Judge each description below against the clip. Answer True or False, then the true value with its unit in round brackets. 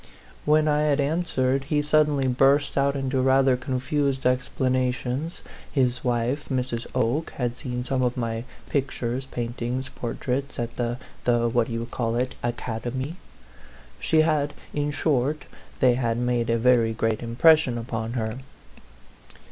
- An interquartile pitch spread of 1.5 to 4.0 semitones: True (2.8 semitones)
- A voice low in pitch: True (130 Hz)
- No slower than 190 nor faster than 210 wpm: False (145 wpm)